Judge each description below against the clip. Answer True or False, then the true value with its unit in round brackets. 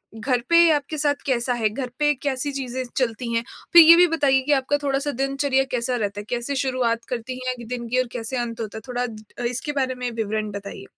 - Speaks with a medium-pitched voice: False (255 Hz)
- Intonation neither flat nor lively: True (3.0 semitones)